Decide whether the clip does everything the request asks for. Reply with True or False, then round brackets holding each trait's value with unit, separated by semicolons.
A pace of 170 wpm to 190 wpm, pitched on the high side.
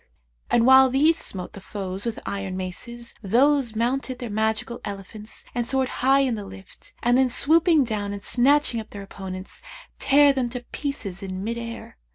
True (180 wpm; 235 Hz)